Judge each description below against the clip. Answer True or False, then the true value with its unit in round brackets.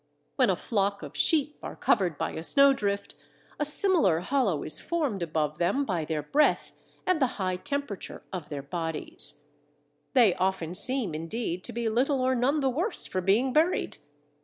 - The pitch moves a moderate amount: False (7.9 semitones)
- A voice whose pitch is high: True (210 Hz)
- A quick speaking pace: False (170 wpm)